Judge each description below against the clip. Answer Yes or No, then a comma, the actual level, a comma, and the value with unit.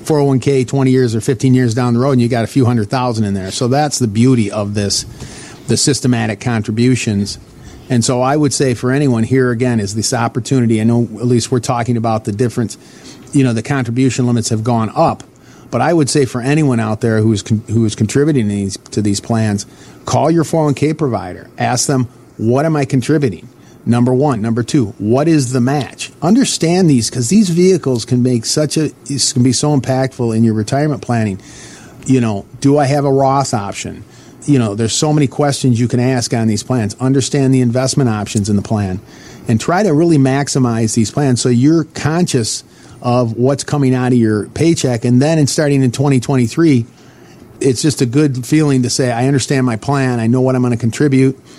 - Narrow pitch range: No, average, 3.4 semitones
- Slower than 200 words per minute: No, fast, 205 wpm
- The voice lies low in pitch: Yes, low, 125 Hz